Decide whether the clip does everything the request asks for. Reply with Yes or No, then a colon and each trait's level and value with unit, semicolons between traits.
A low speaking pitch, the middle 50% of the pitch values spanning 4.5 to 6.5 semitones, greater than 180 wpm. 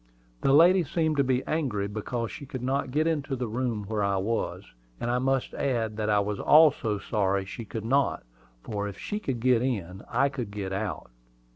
Yes: low, 120 Hz; average, 4.8 semitones; average, 200 wpm